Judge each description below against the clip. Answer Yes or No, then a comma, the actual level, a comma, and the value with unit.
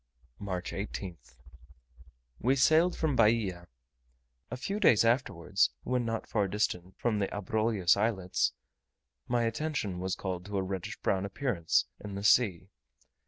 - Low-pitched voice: Yes, low, 105 Hz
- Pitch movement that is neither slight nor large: Yes, average, 4.0 semitones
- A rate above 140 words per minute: No, slow, 135 wpm